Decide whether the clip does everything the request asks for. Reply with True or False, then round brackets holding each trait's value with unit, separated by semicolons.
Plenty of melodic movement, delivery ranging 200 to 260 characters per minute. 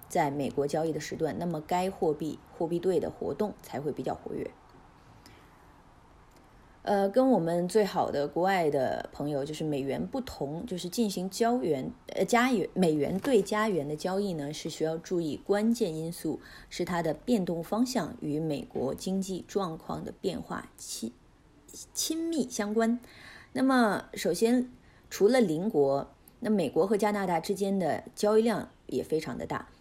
True (5.7 semitones; 240 characters per minute)